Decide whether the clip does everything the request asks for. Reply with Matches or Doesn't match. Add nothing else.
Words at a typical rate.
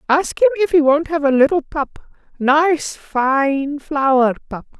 Matches